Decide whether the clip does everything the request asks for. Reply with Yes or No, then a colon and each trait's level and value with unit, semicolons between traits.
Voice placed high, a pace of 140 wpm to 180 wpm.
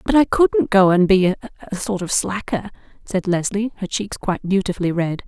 No: high, 195 Hz; average, 195 wpm